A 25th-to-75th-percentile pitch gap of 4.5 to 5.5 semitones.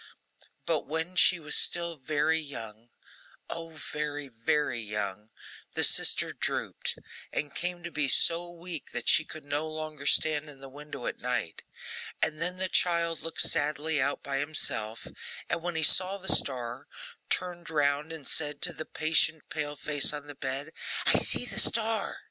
No: average, 2.8 semitones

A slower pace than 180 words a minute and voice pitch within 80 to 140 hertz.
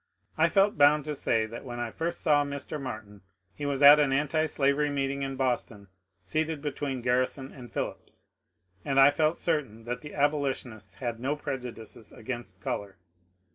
Yes: average, 165 wpm; low, 135 Hz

